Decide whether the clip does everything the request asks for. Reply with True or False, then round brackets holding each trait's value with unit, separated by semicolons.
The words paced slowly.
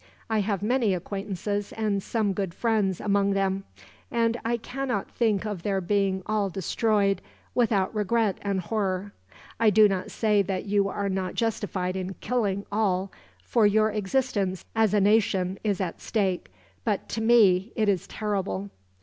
False (160 wpm)